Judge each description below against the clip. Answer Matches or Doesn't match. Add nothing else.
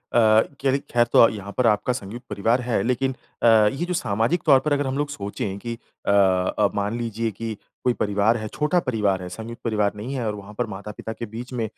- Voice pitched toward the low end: Matches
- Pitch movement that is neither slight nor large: Matches